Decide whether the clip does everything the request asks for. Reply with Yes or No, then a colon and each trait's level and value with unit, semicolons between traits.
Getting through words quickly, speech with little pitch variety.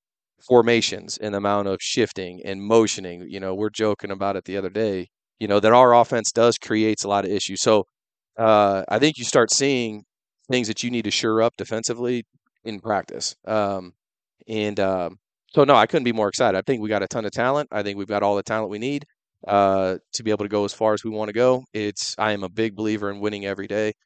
Yes: fast, 235 wpm; narrow, 2.3 semitones